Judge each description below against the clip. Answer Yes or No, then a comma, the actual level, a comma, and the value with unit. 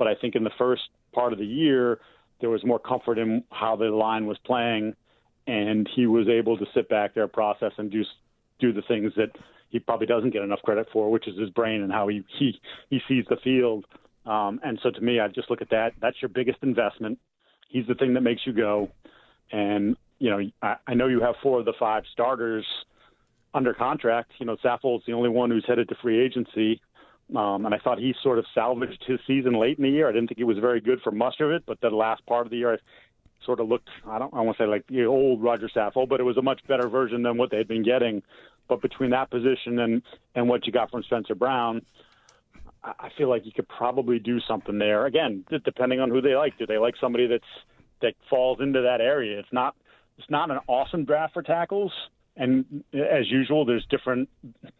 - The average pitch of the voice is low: Yes, low, 120 Hz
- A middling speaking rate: No, fast, 230 wpm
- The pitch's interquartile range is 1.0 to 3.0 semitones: Yes, narrow, 2.4 semitones